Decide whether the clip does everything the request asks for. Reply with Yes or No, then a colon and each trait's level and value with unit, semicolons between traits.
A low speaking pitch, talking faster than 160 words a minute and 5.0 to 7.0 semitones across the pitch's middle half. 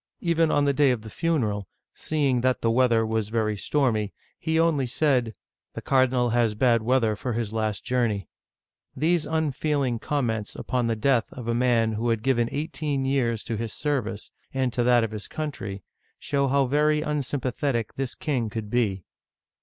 No: low, 125 Hz; average, 185 wpm; average, 3.9 semitones